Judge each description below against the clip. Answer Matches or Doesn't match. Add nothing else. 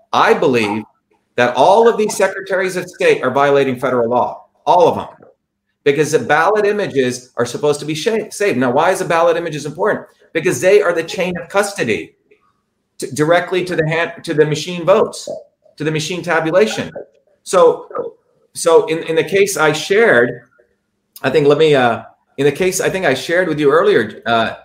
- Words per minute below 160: Doesn't match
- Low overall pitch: Doesn't match